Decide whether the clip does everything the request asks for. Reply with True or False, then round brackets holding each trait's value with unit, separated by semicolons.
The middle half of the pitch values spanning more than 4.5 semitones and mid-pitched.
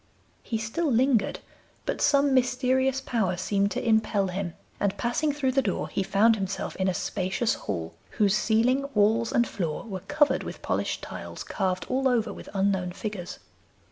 False (4.9 semitones; 220 Hz)